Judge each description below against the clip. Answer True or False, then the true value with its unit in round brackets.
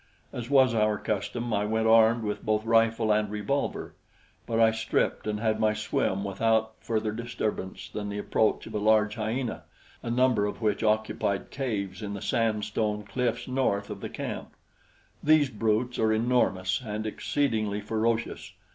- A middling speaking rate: True (165 wpm)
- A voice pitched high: False (110 Hz)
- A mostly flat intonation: True (1.6 semitones)